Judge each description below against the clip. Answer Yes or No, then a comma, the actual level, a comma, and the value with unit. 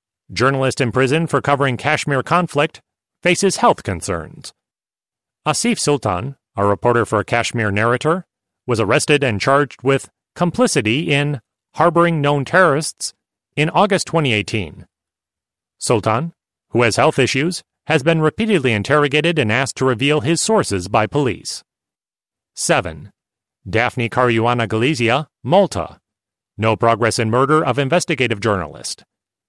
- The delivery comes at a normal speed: No, slow, 120 wpm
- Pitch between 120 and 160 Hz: Yes, low, 135 Hz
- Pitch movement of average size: No, wide, 5.7 semitones